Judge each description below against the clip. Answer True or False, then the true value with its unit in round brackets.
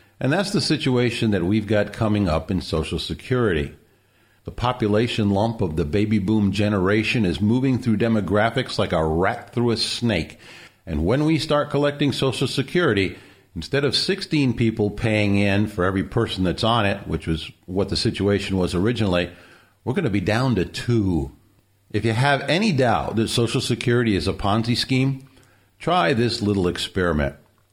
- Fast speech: False (170 wpm)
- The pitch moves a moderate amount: True (4.0 semitones)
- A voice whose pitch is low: True (110 Hz)